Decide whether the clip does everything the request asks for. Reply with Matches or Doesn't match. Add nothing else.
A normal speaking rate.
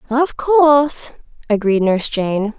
Doesn't match